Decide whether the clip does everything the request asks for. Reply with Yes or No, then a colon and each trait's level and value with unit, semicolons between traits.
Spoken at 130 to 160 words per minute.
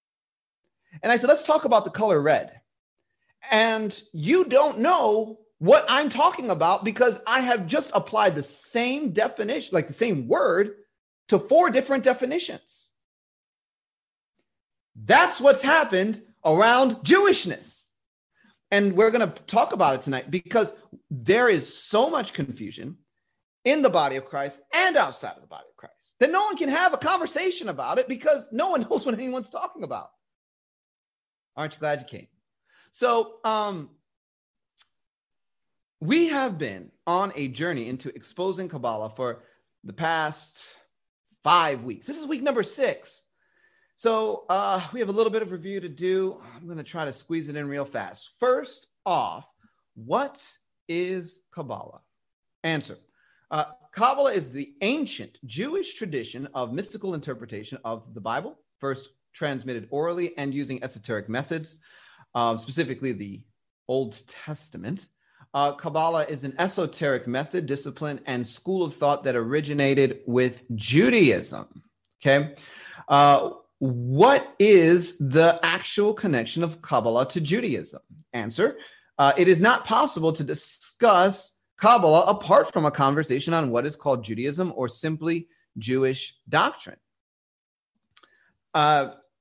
Yes: average, 140 wpm